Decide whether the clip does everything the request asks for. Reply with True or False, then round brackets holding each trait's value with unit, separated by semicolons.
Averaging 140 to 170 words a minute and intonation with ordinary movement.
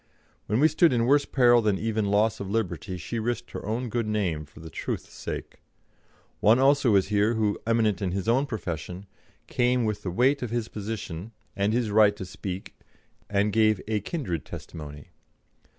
False (180 wpm; 3.5 semitones)